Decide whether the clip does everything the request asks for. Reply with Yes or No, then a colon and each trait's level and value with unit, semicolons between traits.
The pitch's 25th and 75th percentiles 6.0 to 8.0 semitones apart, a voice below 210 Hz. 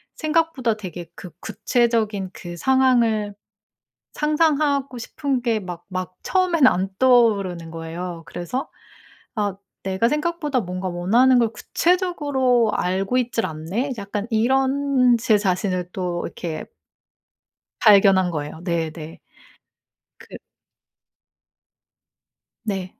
No: wide, 6.3 semitones; high, 215 Hz